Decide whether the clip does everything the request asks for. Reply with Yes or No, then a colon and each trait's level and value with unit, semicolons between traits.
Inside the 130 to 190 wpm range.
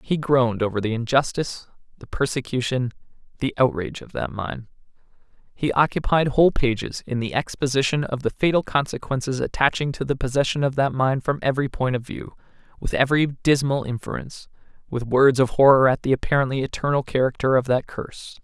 Yes: average, 165 wpm